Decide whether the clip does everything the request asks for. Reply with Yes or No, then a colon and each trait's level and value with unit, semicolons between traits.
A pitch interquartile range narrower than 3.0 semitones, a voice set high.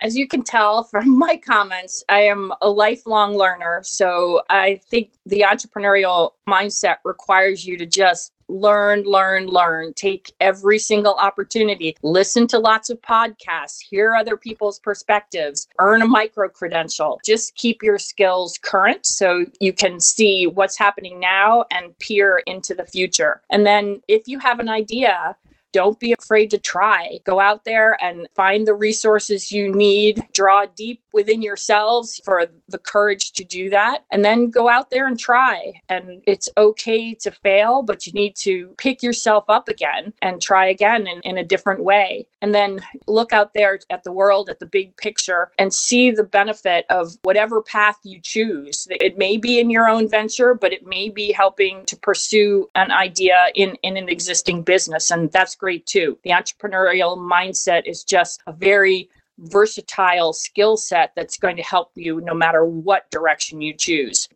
Yes: narrow, 2.6 semitones; high, 200 Hz